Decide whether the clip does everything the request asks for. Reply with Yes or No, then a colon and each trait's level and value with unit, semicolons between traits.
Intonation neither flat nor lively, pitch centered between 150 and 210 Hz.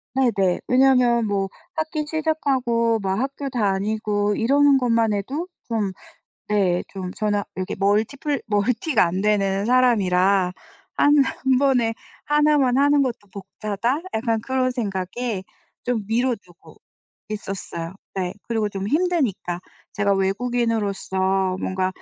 No: average, 4.7 semitones; high, 220 Hz